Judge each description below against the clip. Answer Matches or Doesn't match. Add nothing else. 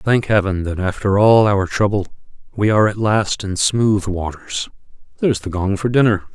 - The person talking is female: Doesn't match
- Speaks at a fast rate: Doesn't match